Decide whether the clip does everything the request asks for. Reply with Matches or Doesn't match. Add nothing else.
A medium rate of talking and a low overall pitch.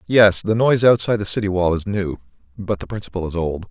Doesn't match